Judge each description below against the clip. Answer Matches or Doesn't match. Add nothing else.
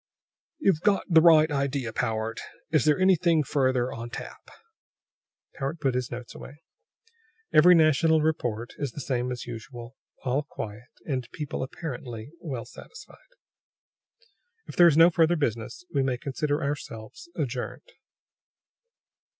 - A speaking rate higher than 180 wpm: Doesn't match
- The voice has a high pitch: Doesn't match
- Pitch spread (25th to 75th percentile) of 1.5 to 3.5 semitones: Doesn't match